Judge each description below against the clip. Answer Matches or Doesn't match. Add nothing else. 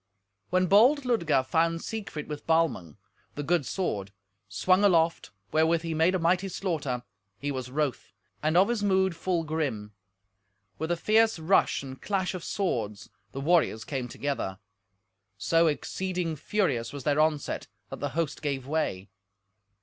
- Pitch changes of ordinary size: Matches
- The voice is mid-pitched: Matches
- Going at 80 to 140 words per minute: Doesn't match